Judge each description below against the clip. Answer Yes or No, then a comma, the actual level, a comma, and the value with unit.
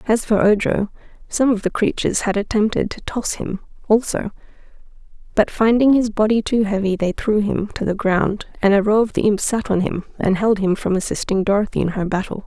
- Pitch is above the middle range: Yes, high, 205 Hz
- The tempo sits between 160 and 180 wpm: No, fast, 205 wpm